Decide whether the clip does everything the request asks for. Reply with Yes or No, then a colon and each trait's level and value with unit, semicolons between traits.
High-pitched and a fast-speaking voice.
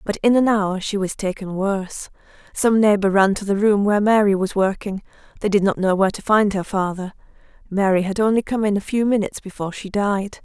Yes: high, 200 Hz; fast, 220 wpm